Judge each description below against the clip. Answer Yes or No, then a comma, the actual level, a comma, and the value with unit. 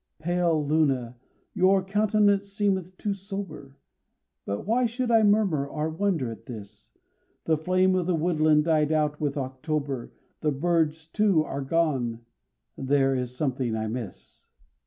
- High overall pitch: No, medium, 155 Hz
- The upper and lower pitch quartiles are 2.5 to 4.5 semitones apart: No, wide, 5.6 semitones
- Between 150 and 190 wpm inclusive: No, average, 140 wpm